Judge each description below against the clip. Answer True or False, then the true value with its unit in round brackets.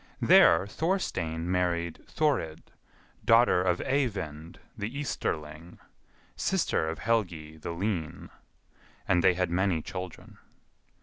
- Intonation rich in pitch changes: False (4.0 semitones)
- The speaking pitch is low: True (90 Hz)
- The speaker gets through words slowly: True (105 wpm)